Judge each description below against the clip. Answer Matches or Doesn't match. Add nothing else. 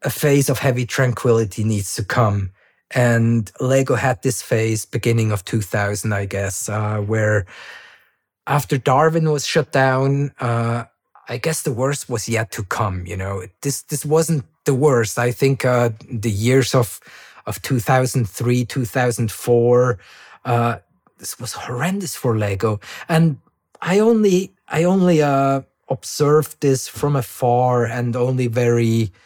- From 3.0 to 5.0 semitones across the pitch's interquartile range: Matches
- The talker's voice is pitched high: Doesn't match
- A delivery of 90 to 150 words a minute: Matches